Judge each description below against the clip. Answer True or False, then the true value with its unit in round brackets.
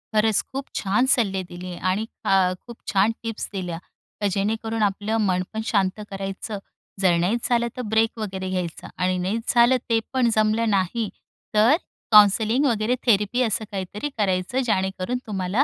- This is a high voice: True (210 Hz)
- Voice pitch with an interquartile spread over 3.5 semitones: False (3.2 semitones)